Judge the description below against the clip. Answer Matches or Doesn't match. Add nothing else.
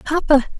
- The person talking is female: Matches